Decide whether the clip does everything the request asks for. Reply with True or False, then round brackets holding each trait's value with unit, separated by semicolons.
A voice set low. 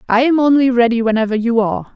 False (240 Hz)